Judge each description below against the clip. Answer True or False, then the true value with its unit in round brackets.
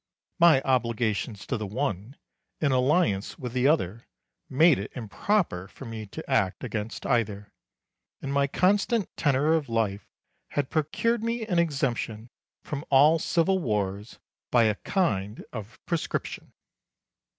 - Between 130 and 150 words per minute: True (135 wpm)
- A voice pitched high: False (130 Hz)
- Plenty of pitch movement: True (6.9 semitones)